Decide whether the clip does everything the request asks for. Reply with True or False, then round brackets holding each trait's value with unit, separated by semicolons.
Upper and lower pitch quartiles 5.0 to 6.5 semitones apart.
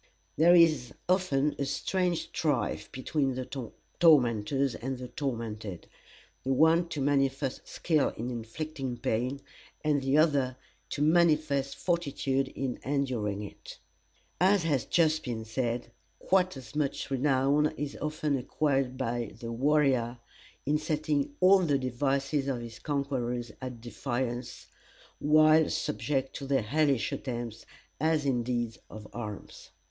False (3.7 semitones)